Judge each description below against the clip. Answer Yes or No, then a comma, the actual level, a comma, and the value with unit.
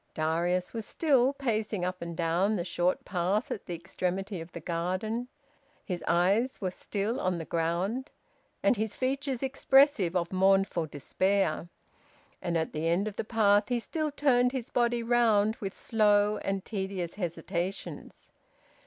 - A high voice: Yes, high, 195 Hz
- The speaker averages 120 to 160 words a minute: Yes, average, 155 wpm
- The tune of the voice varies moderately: Yes, average, 4.8 semitones